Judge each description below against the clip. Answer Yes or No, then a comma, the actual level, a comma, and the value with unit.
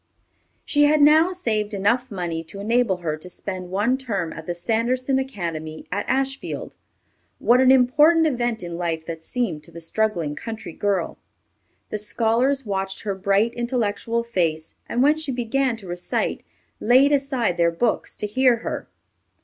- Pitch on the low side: No, high, 220 Hz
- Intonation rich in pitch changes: Yes, wide, 6.3 semitones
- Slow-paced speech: No, average, 160 wpm